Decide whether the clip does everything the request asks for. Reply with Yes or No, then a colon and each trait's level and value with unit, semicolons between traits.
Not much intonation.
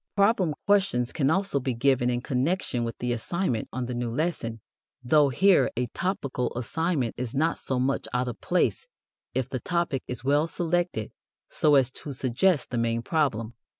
No: wide, 5.5 semitones